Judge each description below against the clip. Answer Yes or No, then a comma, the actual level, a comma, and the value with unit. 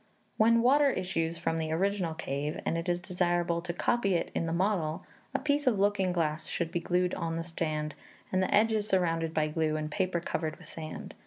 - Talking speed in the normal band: No, fast, 210 wpm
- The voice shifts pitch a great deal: No, average, 3.0 semitones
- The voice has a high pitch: No, medium, 175 Hz